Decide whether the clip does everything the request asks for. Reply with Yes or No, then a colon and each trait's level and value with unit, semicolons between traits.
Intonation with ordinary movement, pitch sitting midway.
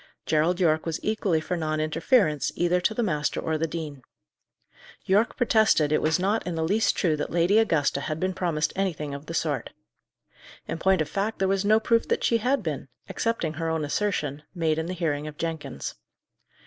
Yes: average, 4.2 semitones; medium, 165 Hz